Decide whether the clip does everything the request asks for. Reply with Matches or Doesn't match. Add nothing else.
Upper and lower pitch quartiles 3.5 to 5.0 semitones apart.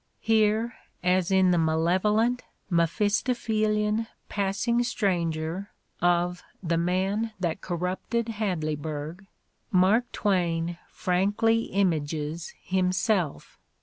Matches